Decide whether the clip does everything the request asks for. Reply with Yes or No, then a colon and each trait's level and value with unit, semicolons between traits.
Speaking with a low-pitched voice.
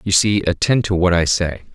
Yes: very low, 95 Hz